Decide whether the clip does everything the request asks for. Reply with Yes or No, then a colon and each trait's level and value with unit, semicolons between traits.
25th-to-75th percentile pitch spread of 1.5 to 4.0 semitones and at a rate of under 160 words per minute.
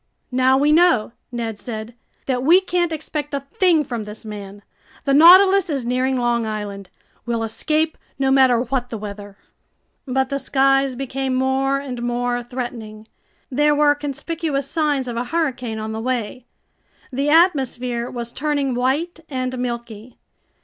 Yes: average, 3.4 semitones; average, 150 wpm